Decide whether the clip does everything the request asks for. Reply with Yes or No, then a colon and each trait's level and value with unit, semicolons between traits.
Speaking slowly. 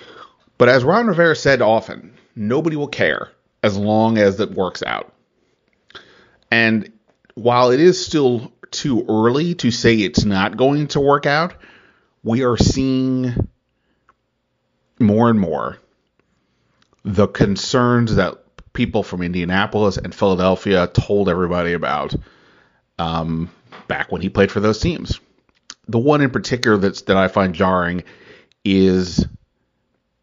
Yes: slow, 130 wpm